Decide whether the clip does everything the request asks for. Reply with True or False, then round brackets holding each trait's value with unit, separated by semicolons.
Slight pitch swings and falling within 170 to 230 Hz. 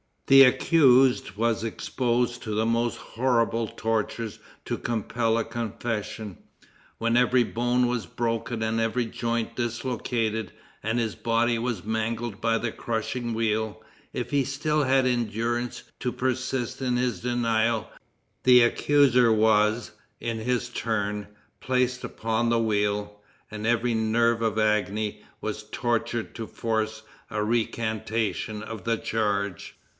False (1.7 semitones; 115 Hz)